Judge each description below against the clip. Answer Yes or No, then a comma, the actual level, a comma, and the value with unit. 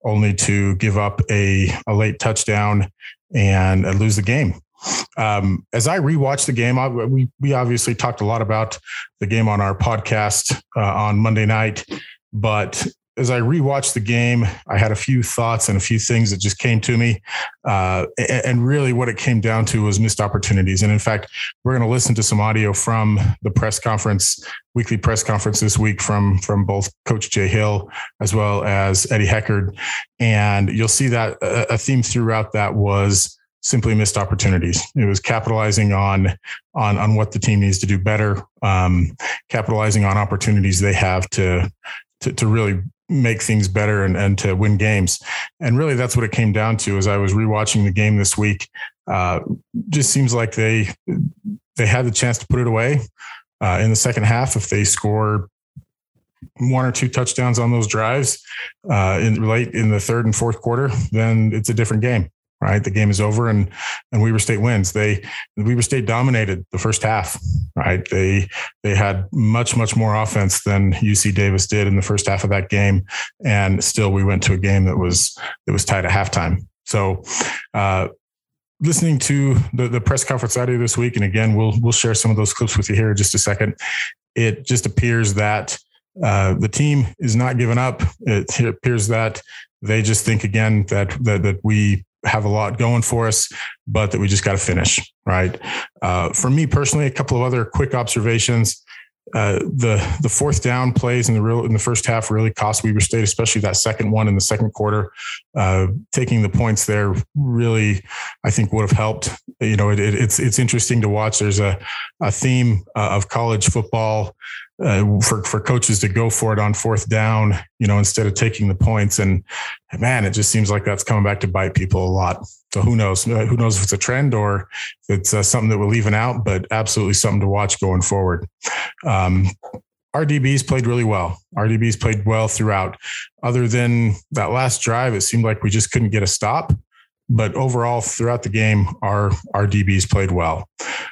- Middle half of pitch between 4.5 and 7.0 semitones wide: No, average, 2.7 semitones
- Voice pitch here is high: No, low, 110 Hz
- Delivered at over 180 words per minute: Yes, average, 195 wpm